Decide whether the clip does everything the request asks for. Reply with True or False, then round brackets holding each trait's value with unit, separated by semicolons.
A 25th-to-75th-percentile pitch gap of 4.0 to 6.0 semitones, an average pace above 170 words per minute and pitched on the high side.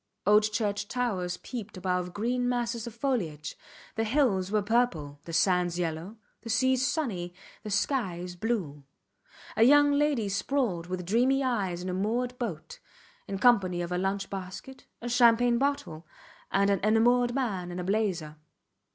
False (5.2 semitones; 155 wpm; 210 Hz)